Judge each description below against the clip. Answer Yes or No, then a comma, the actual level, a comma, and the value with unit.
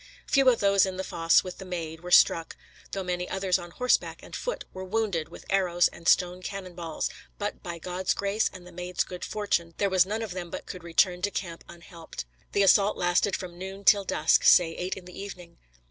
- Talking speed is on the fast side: Yes, fast, 220 wpm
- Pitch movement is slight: Yes, narrow, 2.2 semitones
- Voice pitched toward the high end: No, medium, 180 Hz